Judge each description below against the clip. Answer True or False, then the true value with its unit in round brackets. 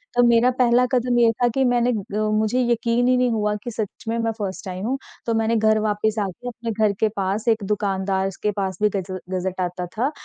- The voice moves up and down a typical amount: True (3.2 semitones)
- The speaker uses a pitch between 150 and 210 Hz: False (220 Hz)